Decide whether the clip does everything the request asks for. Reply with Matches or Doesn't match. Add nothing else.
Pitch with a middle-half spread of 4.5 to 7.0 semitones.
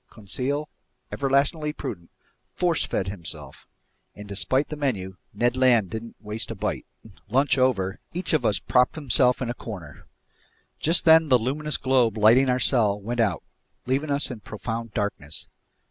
Matches